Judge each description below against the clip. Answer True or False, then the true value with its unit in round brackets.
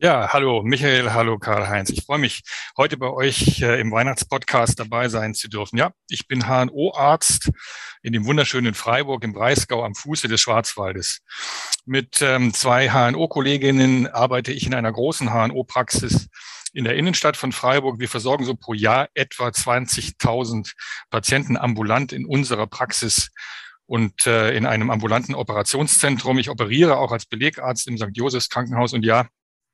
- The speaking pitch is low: True (125 Hz)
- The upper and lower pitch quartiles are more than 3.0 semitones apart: False (2.7 semitones)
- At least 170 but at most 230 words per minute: False (155 wpm)